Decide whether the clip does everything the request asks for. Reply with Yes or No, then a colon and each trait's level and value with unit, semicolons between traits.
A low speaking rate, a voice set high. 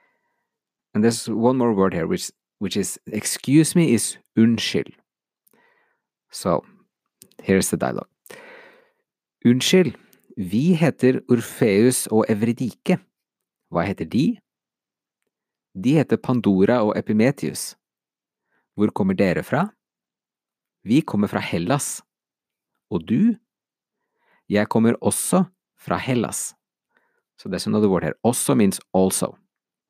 No: slow, 120 wpm; low, 130 Hz